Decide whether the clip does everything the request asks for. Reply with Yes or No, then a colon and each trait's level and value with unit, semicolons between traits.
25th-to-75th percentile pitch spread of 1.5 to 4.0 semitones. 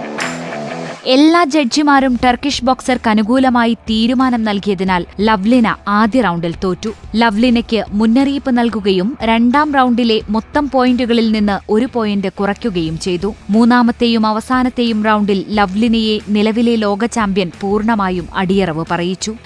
Yes: average, 3.2 semitones